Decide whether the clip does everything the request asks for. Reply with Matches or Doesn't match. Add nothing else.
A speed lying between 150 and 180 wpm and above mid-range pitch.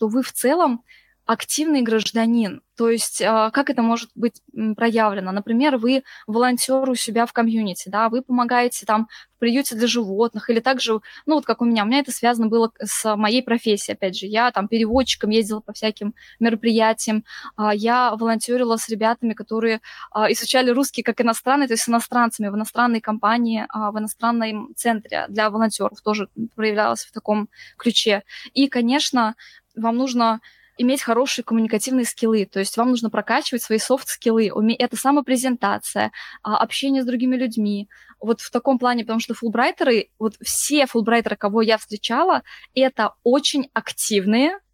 Matches